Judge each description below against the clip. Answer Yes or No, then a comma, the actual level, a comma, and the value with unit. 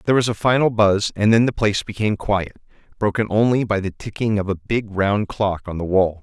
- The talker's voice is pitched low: Yes, low, 105 Hz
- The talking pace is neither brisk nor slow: No, fast, 230 wpm